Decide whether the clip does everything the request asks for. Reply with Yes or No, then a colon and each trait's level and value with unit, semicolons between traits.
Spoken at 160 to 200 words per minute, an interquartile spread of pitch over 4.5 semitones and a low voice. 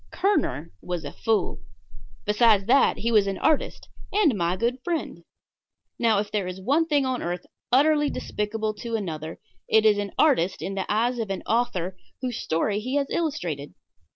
No: average, 175 wpm; average, 5.3 semitones; high, 215 Hz